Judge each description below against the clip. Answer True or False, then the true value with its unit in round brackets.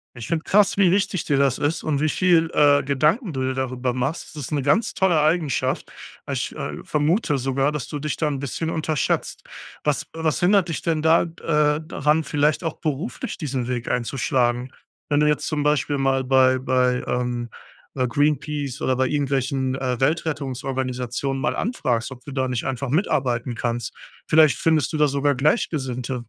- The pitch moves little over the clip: False (3.2 semitones)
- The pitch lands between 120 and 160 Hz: True (140 Hz)